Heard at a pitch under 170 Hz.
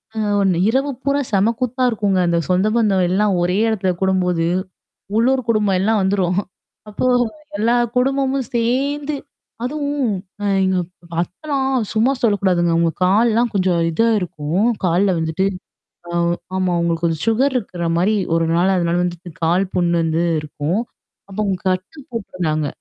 No: high, 195 Hz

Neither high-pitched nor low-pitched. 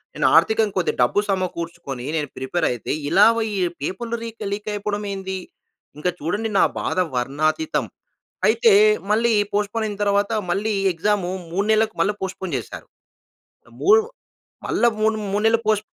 No: high, 205 Hz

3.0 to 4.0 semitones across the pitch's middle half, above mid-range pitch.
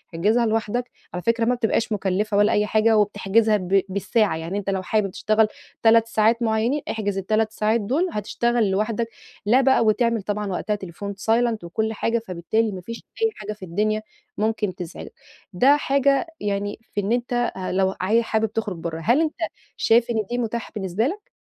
No: narrow, 2.6 semitones; high, 215 Hz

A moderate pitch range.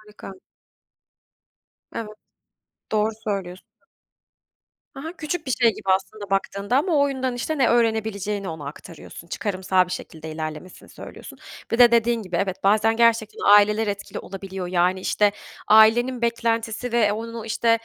Yes: average, 3.4 semitones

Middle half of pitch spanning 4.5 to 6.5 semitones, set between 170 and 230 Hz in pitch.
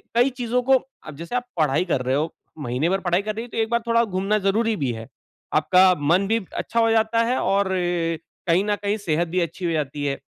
Yes: average, 5.3 semitones; high, 190 Hz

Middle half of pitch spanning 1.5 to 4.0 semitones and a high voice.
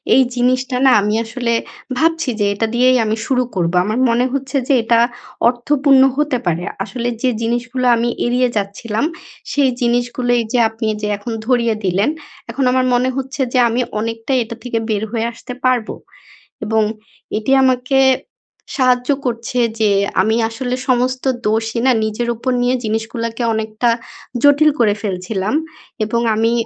Yes: narrow, 2.4 semitones; high, 240 Hz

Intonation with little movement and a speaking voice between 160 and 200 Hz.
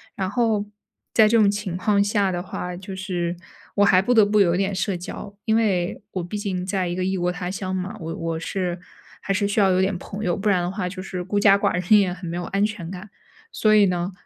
Yes: narrow, 2.2 semitones; high, 190 Hz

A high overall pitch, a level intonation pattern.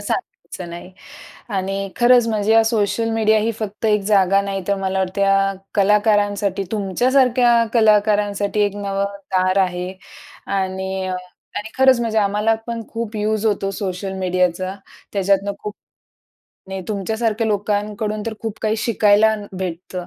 Yes: high, 205 Hz; narrow, 2.2 semitones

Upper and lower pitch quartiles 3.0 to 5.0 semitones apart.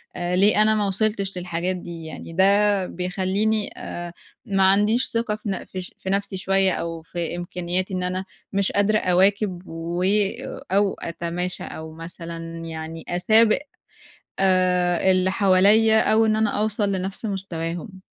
No: narrow, 2.6 semitones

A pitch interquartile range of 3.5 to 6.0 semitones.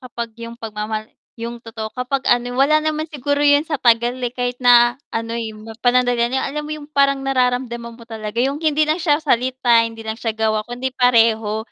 No: average, 3.1 semitones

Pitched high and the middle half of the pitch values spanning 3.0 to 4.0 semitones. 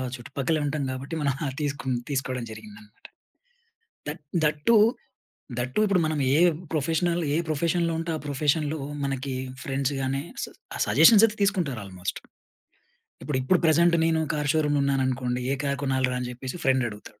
No: medium, 145 Hz; average, 3.7 semitones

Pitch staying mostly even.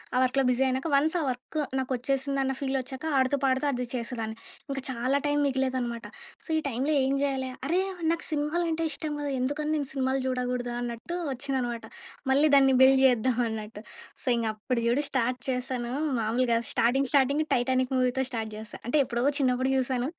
Yes: narrow, 2.1 semitones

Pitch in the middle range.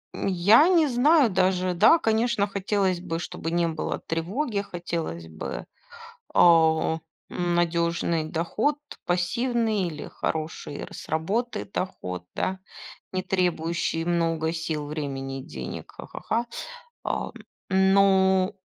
Yes: medium, 175 Hz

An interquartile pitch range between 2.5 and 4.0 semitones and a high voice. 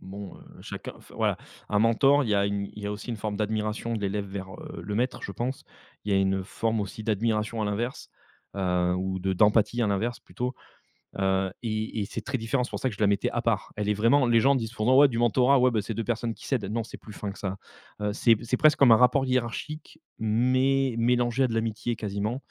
No: average, 3.1 semitones; low, 110 Hz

